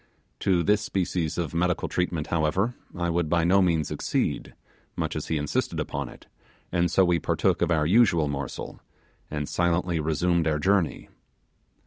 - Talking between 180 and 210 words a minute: No, average, 160 wpm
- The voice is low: Yes, very low, 85 Hz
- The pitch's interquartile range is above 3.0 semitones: No, narrow, 2.4 semitones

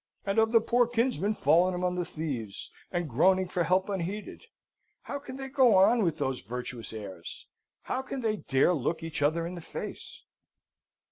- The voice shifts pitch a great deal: Yes, wide, 6.6 semitones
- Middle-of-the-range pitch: Yes, medium, 180 Hz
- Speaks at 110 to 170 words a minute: No, average, 180 wpm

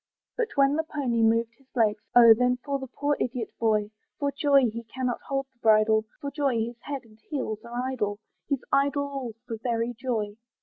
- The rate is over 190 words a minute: Yes, average, 200 wpm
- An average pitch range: Yes, average, 3.6 semitones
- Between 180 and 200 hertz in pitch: No, high, 245 Hz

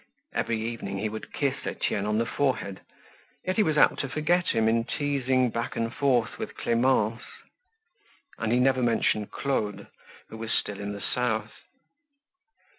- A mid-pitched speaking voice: No, low, 115 Hz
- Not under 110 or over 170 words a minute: Yes, average, 160 wpm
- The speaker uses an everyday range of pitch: Yes, average, 3.4 semitones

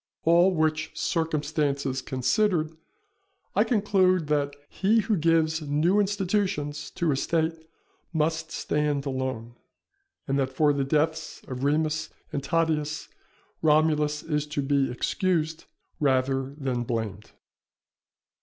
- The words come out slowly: Yes, slow, 115 wpm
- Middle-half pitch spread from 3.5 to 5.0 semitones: No, average, 2.8 semitones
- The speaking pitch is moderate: Yes, medium, 150 Hz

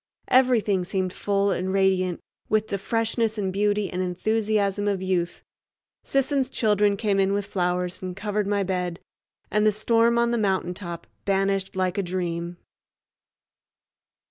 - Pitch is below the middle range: No, high, 195 Hz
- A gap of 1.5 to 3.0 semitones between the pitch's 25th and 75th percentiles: Yes, narrow, 2.4 semitones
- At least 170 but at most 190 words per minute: No, average, 145 wpm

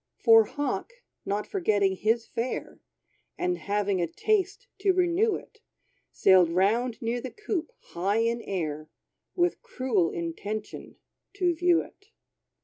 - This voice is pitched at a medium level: No, high, 230 Hz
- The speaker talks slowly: Yes, slow, 130 wpm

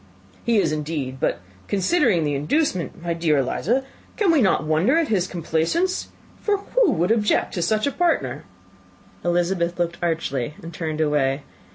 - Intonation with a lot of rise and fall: Yes, wide, 6.9 semitones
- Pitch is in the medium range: Yes, medium, 175 Hz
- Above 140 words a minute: Yes, average, 160 wpm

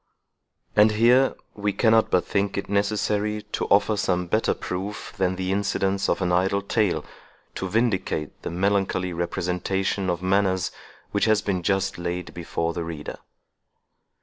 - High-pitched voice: No, very low, 95 Hz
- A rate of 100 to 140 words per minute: No, average, 150 wpm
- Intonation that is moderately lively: No, narrow, 2.3 semitones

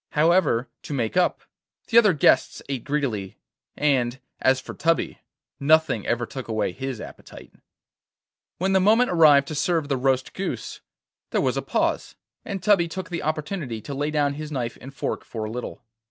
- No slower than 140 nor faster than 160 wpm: No, average, 175 wpm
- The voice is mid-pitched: Yes, medium, 145 Hz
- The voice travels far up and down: No, average, 4.5 semitones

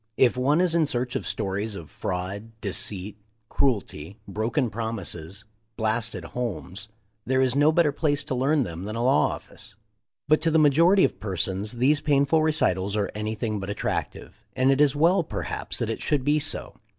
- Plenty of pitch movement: Yes, wide, 6.2 semitones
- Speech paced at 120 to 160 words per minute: No, average, 175 wpm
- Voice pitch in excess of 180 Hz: No, low, 120 Hz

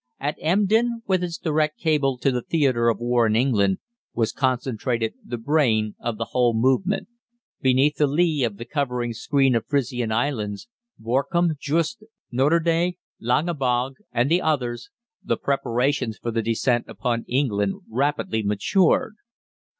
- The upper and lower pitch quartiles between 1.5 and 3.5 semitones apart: No, average, 4.5 semitones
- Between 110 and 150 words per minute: Yes, average, 140 wpm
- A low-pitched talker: Yes, low, 130 Hz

